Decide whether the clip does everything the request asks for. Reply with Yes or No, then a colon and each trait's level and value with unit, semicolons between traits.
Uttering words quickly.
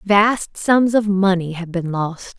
No: average, 175 wpm